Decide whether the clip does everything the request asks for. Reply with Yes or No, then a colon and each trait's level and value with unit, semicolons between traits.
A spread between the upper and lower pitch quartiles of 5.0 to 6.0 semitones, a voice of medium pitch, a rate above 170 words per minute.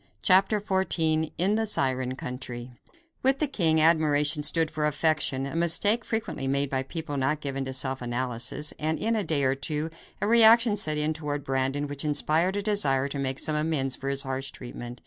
No: average, 3.8 semitones; medium, 150 Hz; average, 190 wpm